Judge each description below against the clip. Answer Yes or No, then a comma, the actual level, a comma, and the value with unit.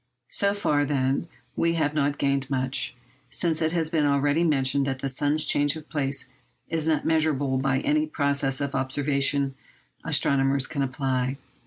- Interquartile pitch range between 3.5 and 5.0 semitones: No, narrow, 2.4 semitones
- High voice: No, medium, 140 Hz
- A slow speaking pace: No, average, 160 wpm